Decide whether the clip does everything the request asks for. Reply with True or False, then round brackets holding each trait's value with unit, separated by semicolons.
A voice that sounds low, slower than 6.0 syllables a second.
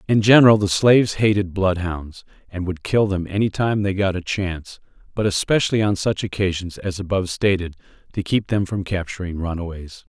True (95 Hz; 5.5 syllables/s)